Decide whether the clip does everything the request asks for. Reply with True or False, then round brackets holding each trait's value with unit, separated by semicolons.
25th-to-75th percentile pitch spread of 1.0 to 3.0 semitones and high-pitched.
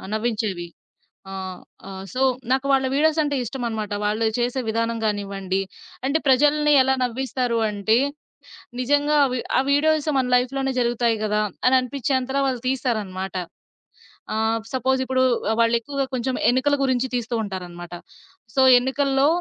False (3.4 semitones; 250 Hz)